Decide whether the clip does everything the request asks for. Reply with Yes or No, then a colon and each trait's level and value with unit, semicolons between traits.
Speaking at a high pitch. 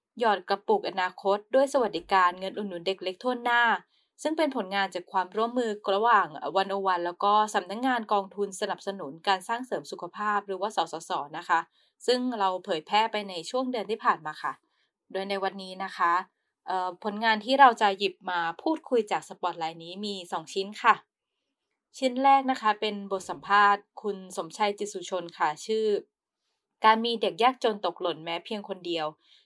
Yes: high, 200 Hz